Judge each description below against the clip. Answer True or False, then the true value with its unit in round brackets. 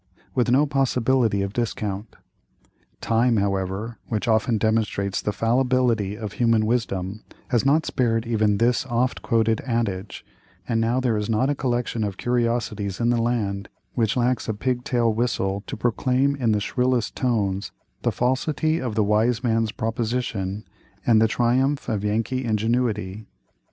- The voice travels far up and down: False (2.6 semitones)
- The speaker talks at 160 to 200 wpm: False (150 wpm)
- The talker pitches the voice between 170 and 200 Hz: False (115 Hz)